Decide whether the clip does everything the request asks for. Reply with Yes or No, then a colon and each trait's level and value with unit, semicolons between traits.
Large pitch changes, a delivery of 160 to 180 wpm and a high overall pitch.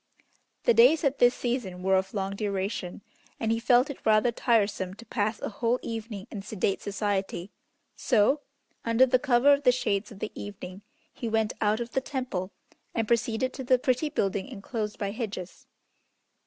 No: average, 3.8 semitones; average, 175 wpm; high, 220 Hz